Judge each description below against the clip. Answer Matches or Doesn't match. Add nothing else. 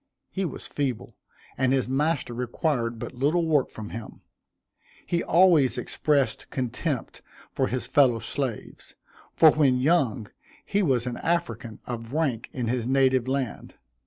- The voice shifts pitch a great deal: Doesn't match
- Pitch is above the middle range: Doesn't match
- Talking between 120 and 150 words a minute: Matches